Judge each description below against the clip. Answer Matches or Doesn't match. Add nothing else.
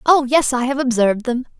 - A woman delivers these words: Matches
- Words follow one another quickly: Matches